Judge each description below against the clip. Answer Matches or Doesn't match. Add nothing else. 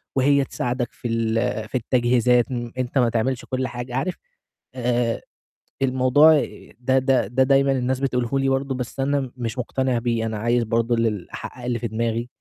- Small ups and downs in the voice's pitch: Matches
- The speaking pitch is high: Doesn't match